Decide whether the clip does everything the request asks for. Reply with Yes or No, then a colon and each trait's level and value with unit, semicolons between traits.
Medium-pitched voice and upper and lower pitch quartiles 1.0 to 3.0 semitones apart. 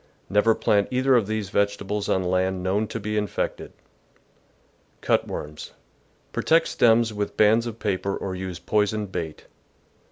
No: low, 105 Hz; narrow, 2.6 semitones